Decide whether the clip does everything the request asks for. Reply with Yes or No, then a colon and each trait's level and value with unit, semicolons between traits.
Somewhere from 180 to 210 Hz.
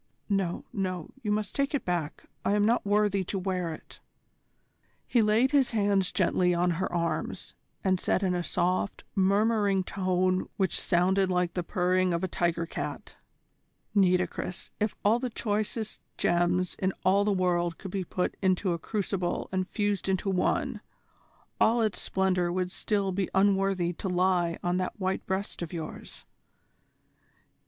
Yes: medium, 185 Hz